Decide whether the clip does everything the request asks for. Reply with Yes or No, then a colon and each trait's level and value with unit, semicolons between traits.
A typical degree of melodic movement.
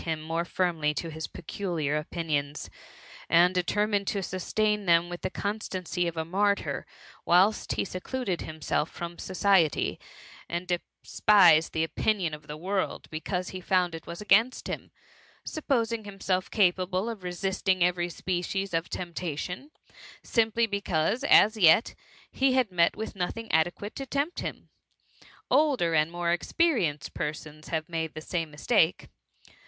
Yes: average, 3.7 semitones